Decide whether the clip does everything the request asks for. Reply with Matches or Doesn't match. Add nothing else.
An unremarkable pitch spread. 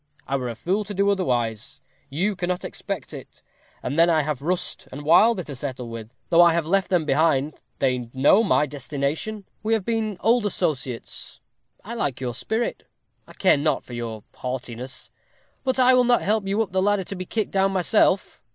Doesn't match